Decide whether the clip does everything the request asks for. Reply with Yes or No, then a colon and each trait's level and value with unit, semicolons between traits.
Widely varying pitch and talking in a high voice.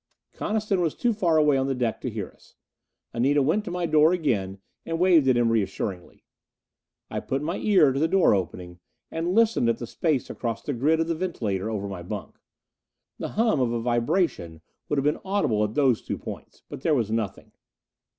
No: wide, 6.9 semitones; low, 135 Hz